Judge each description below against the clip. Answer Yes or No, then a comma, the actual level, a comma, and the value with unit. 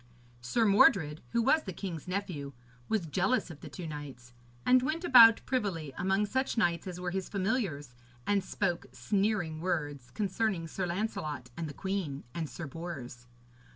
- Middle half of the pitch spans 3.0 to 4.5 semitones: No, average, 5.2 semitones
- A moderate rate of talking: Yes, average, 160 wpm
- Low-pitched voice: No, medium, 180 Hz